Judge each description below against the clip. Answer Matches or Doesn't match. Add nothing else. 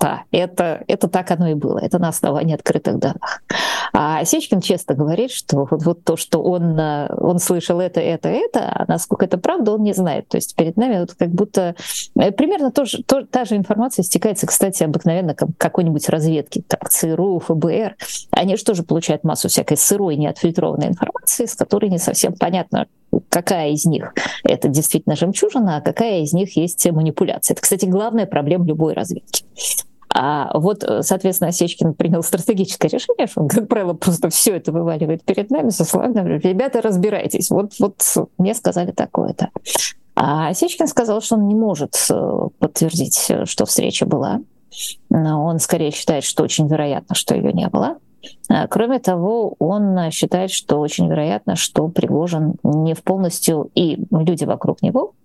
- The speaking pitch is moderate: Matches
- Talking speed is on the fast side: Matches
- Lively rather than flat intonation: Doesn't match